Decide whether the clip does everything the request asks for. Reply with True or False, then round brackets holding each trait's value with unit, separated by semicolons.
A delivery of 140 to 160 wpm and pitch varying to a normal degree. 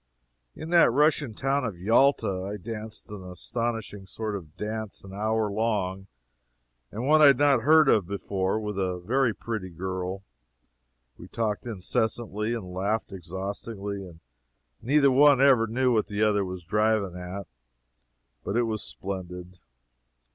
True (155 wpm; 3.6 semitones)